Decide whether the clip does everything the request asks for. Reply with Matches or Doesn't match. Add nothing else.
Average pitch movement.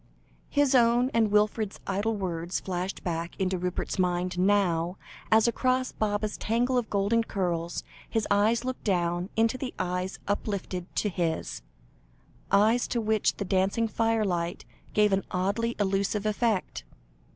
Matches